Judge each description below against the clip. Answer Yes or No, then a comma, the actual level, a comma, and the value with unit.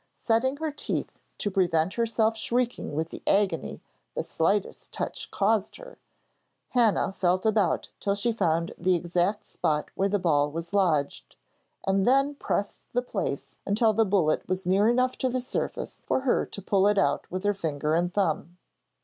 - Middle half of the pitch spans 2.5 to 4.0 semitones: No, average, 4.5 semitones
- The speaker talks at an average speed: Yes, average, 170 wpm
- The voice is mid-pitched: No, high, 200 Hz